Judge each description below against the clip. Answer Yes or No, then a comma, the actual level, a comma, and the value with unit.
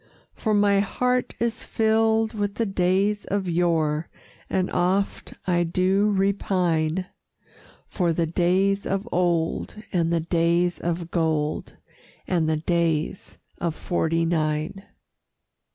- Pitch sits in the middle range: Yes, medium, 180 Hz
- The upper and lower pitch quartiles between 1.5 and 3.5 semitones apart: Yes, average, 3.1 semitones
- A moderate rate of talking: No, slow, 120 wpm